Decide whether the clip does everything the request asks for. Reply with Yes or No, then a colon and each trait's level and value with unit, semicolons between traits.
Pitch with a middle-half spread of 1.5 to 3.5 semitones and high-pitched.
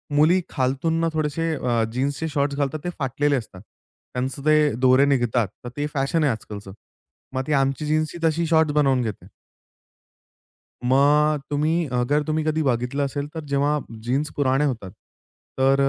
No: average, 2.7 semitones; medium, 140 Hz